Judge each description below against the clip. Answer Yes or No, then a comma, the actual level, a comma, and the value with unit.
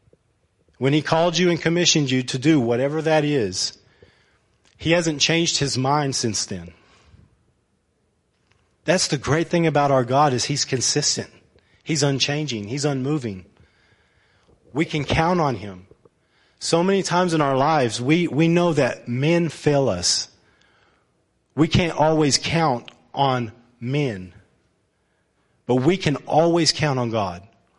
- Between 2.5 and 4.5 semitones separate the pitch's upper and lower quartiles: No, wide, 5.6 semitones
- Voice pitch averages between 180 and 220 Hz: No, medium, 140 Hz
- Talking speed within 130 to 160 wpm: Yes, average, 140 wpm